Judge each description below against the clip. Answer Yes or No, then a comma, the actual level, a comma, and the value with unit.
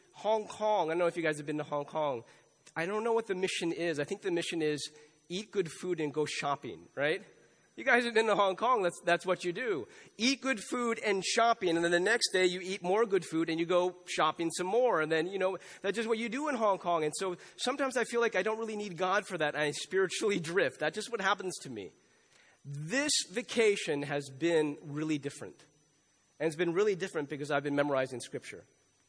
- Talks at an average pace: No, fast, 235 wpm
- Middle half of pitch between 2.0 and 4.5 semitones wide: No, wide, 5.4 semitones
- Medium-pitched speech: Yes, medium, 180 Hz